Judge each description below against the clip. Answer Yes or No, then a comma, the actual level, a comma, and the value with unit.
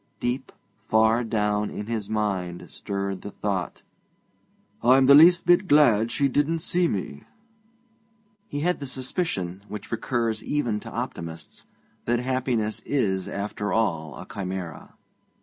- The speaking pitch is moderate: No, low, 110 Hz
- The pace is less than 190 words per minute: Yes, slow, 135 wpm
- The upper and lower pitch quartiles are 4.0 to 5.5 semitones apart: Yes, average, 5.0 semitones